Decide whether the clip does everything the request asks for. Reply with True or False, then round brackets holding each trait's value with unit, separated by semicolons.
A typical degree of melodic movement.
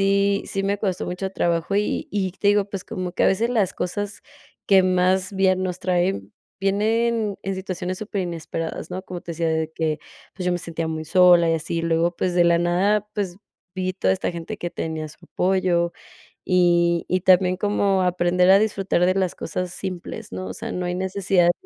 False (2.2 semitones)